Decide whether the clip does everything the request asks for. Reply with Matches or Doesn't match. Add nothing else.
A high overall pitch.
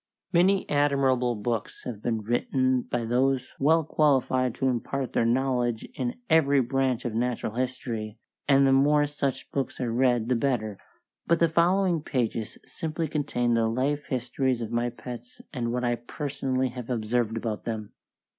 Doesn't match